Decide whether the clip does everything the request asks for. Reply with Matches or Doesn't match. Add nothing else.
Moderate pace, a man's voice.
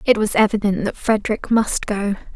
Doesn't match